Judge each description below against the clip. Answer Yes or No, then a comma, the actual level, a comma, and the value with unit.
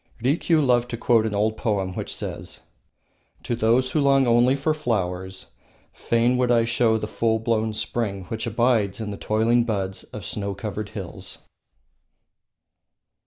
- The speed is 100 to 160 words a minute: Yes, average, 155 wpm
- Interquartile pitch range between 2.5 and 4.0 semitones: Yes, average, 2.8 semitones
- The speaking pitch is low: Yes, low, 115 Hz